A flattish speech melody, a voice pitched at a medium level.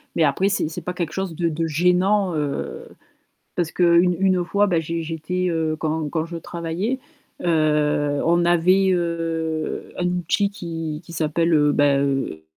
Yes: narrow, 2.3 semitones; medium, 165 Hz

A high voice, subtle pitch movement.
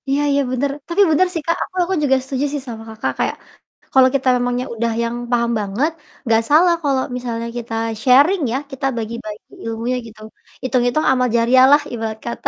No: very high, 250 Hz; average, 3.5 semitones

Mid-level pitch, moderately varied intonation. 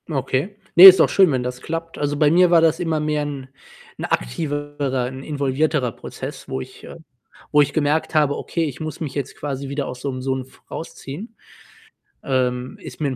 Yes: medium, 145 Hz; average, 3.2 semitones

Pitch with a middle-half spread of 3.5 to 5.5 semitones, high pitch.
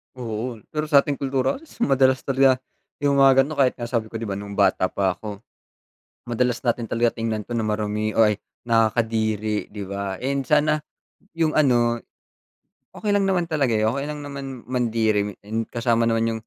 No: average, 3.9 semitones; low, 120 Hz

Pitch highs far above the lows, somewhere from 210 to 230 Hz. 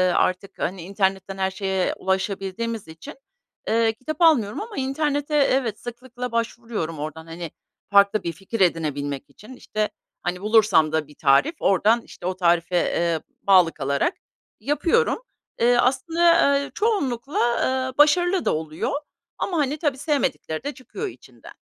Yes: wide, 7.3 semitones; high, 215 Hz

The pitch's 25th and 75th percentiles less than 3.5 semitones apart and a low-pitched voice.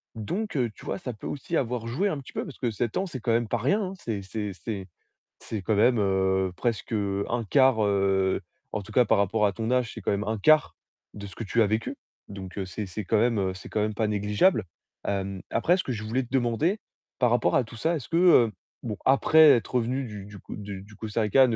No: average, 3.8 semitones; low, 110 Hz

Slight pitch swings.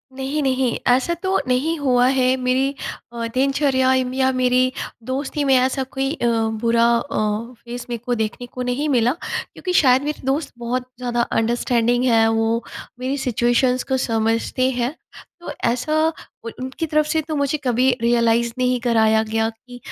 Yes: narrow, 2.1 semitones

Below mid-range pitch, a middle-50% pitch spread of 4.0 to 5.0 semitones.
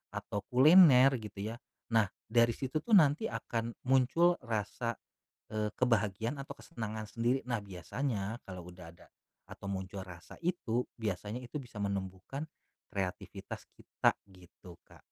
Yes: low, 115 Hz; average, 4.7 semitones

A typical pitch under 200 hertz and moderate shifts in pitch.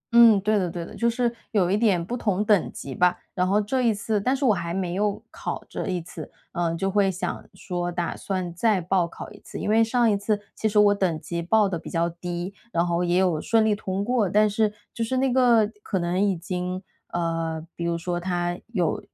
Yes: high, 190 Hz; average, 3.6 semitones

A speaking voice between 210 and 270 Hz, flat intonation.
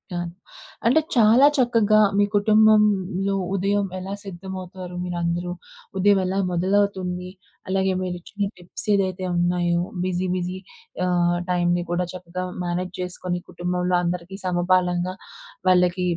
No: medium, 185 Hz; narrow, 1.8 semitones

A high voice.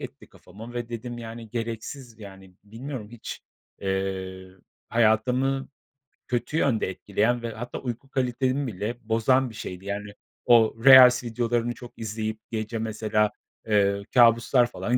No: low, 115 Hz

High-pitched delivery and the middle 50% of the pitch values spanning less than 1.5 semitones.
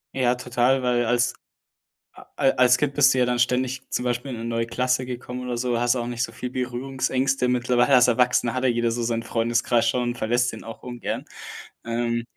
No: low, 125 Hz; narrow, 1.1 semitones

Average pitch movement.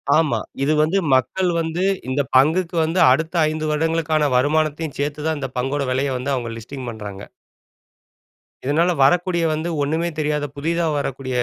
Yes: average, 3.4 semitones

